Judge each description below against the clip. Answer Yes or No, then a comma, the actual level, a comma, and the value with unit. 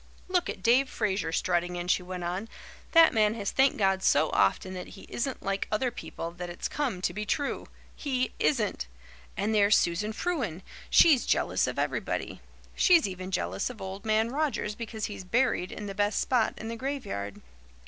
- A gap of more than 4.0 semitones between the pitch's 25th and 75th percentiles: Yes, wide, 5.5 semitones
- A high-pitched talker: Yes, high, 210 Hz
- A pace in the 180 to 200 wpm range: Yes, average, 185 wpm